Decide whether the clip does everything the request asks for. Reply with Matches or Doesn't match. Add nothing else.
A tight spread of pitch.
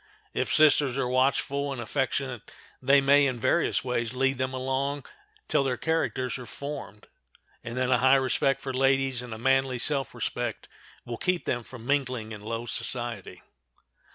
Matches